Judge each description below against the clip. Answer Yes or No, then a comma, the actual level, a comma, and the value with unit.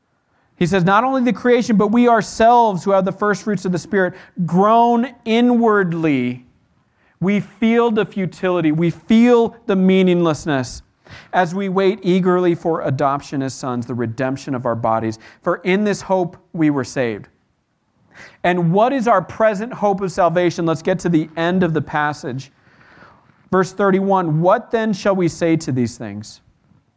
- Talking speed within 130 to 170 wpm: Yes, average, 160 wpm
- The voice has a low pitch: No, medium, 180 Hz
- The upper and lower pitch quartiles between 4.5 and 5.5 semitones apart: Yes, average, 5.0 semitones